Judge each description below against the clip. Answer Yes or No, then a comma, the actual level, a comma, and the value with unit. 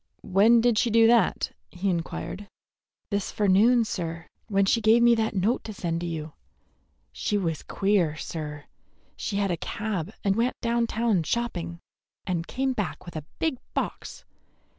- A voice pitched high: Yes, high, 200 Hz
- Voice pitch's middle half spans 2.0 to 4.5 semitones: No, average, 5.1 semitones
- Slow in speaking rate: No, average, 160 wpm